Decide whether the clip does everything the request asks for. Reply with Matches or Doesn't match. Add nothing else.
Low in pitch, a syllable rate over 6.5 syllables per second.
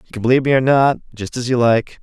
Matches